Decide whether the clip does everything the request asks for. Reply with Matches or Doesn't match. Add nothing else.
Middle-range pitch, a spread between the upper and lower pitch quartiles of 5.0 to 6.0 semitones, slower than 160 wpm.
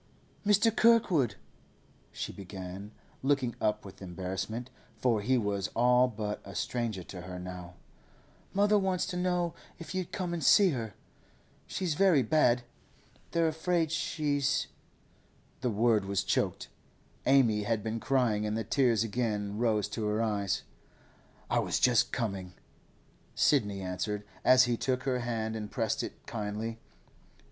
Doesn't match